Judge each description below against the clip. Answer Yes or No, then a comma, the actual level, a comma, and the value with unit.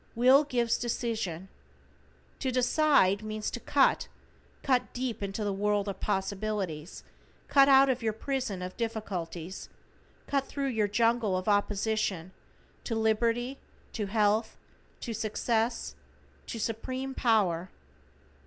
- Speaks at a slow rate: Yes, slow, 120 wpm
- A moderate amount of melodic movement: Yes, average, 3.5 semitones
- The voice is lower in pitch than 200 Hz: No, high, 220 Hz